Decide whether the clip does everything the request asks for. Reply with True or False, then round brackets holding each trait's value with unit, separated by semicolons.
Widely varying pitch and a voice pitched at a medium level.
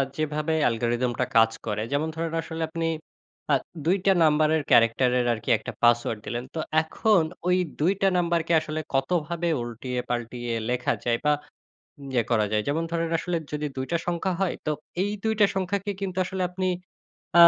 True (6.0 semitones; 155 Hz)